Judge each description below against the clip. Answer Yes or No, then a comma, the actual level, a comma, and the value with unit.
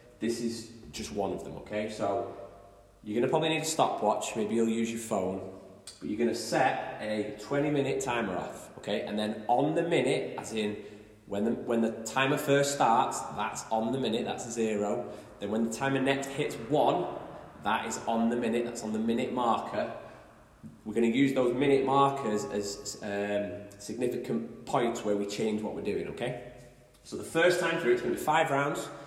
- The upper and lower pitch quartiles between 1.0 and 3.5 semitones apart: No, average, 4.2 semitones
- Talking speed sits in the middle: Yes, average, 195 wpm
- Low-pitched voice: Yes, low, 115 Hz